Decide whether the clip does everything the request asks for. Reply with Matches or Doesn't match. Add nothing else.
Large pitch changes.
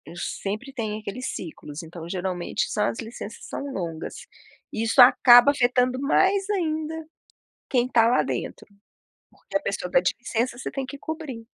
Matches